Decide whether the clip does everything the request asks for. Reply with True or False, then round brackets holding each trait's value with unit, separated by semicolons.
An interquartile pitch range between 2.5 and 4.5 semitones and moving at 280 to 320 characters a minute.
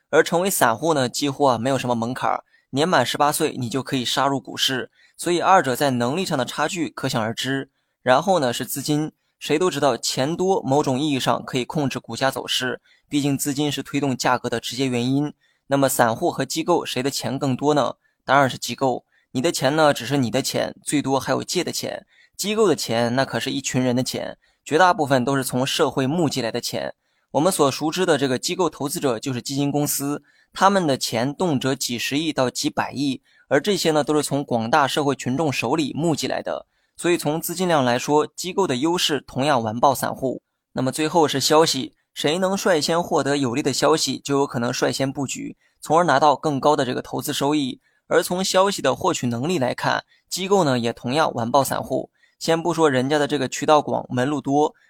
True (3.1 semitones; 315 characters per minute)